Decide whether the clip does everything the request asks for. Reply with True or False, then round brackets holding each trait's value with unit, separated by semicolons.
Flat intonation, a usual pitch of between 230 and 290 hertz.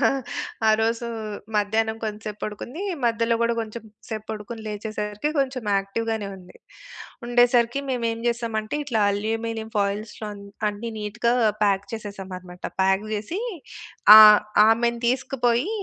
False (2.2 semitones; 220 Hz)